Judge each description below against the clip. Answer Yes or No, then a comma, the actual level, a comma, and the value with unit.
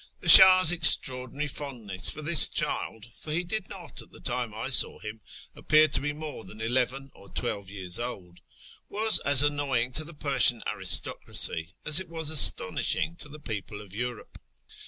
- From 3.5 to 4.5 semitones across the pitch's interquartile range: No, wide, 5.6 semitones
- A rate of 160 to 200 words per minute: Yes, average, 175 wpm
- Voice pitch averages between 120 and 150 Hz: Yes, low, 135 Hz